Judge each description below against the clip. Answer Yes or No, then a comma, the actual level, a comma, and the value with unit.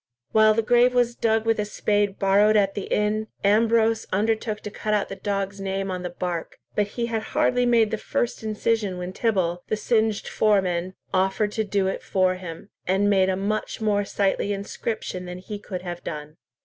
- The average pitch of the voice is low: No, high, 205 Hz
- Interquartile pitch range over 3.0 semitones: No, narrow, 2.5 semitones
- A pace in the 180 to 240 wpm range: Yes, average, 195 wpm